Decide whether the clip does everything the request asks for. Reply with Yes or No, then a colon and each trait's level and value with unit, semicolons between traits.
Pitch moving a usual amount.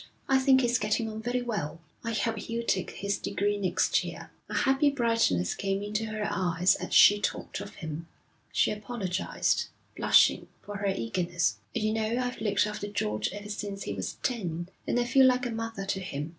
Yes: average, 3.8 semitones